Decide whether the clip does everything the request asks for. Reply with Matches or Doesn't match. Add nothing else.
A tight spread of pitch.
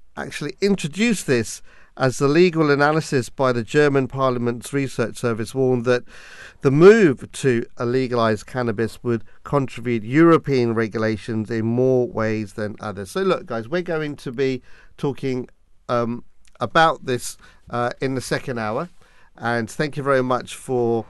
Doesn't match